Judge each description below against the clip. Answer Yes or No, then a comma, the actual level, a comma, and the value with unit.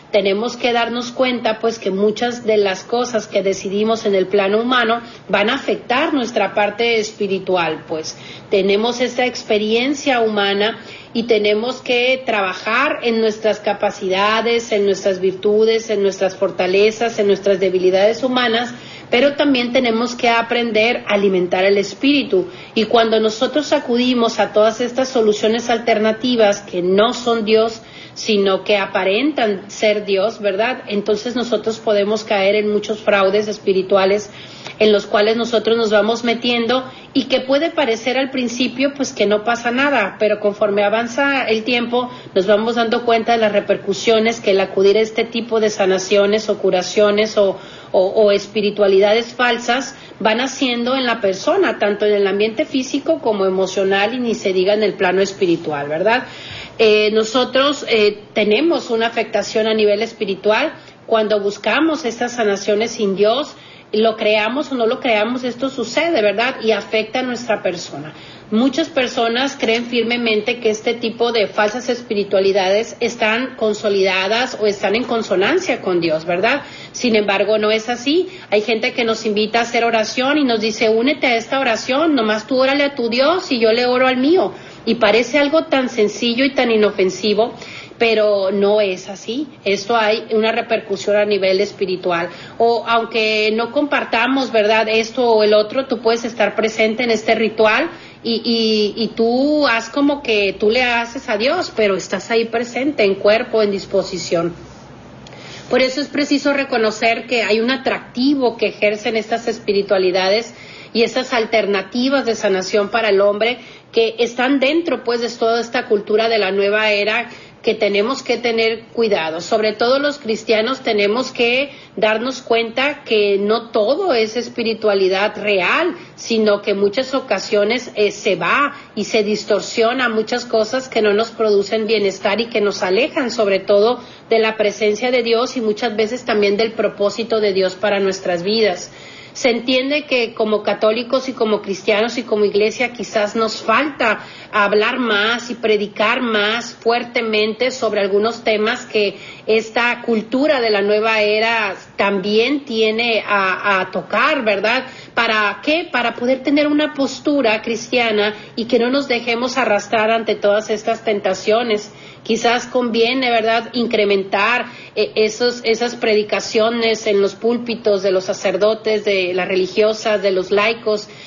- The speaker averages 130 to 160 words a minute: Yes, average, 155 wpm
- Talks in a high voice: Yes, high, 220 Hz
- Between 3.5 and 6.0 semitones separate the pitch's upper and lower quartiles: No, average, 2.7 semitones